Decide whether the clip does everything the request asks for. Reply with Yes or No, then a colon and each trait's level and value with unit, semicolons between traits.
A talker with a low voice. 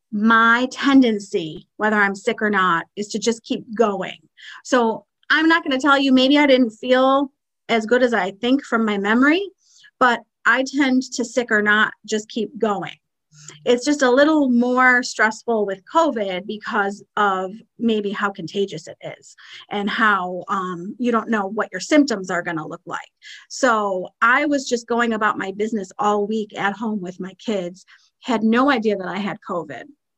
No: high, 220 Hz